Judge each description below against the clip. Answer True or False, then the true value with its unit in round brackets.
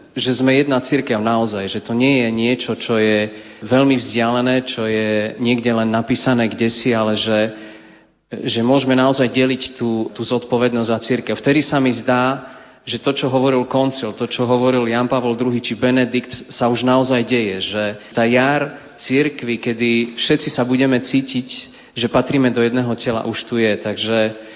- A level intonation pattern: True (2.3 semitones)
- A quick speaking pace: True (175 wpm)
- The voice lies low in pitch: True (120 Hz)